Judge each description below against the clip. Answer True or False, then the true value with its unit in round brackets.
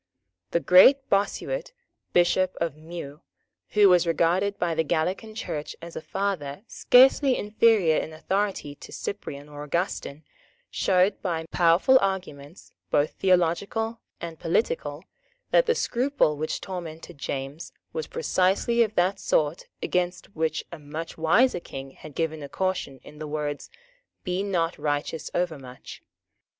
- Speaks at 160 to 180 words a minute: False (135 wpm)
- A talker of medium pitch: True (175 Hz)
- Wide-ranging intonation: False (4.4 semitones)